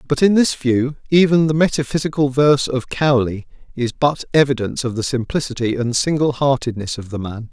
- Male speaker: Yes, male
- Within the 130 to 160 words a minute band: No, average, 175 wpm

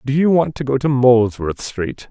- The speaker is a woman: No, male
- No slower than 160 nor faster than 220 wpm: No, fast, 230 wpm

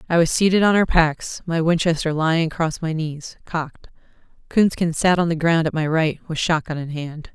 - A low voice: No, medium, 160 Hz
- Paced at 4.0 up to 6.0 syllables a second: Yes, 5.1 syllables/s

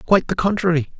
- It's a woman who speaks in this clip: No, male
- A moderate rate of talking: Yes, average, 180 wpm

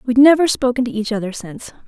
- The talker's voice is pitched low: No, high, 240 Hz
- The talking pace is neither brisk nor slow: No, fast, 225 wpm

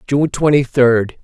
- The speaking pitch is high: No, low, 135 Hz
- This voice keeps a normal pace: Yes, average, 145 wpm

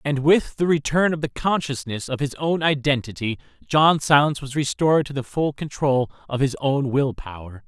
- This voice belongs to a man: Yes, male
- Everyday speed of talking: Yes, average, 190 wpm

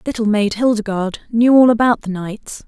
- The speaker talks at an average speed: Yes, average, 180 wpm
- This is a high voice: Yes, high, 220 Hz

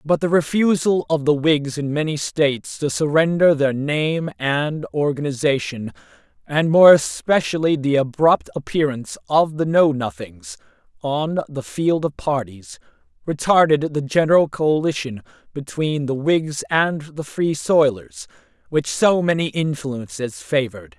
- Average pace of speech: No, slow, 130 wpm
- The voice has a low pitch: No, medium, 150 Hz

